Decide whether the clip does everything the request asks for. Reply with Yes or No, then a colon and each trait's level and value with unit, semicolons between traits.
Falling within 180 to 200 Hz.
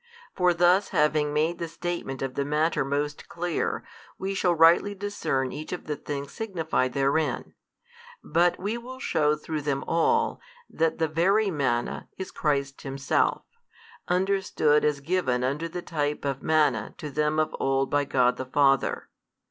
No: medium, 155 Hz